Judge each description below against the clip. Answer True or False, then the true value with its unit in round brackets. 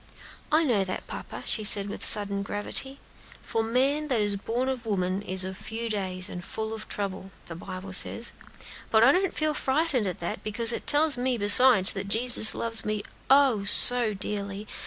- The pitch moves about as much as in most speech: True (4.0 semitones)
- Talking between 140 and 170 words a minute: False (185 wpm)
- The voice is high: True (215 Hz)